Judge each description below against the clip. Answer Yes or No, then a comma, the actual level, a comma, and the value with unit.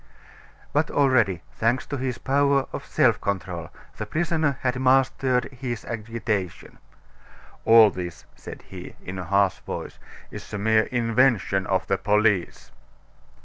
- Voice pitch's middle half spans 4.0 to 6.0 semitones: Yes, average, 5.0 semitones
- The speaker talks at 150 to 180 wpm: No, slow, 135 wpm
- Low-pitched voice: Yes, low, 115 Hz